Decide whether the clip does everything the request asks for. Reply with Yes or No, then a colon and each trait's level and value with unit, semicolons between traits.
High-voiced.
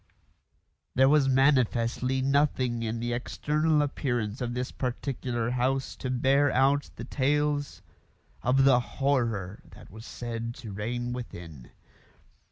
No: low, 125 Hz